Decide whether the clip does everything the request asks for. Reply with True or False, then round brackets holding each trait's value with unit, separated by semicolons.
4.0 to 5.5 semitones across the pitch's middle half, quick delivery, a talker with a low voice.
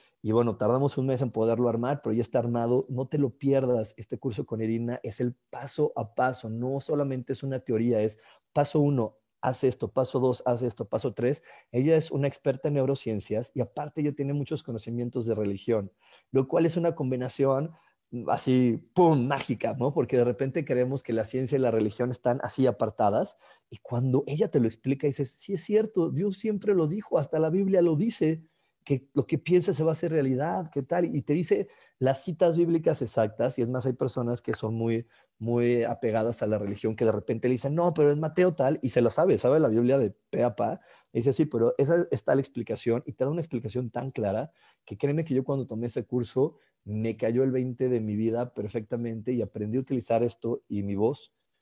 False (3.6 semitones; 215 wpm; 130 Hz)